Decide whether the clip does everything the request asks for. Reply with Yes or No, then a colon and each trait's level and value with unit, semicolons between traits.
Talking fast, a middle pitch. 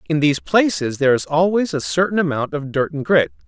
Yes: fast, 225 wpm; medium, 155 Hz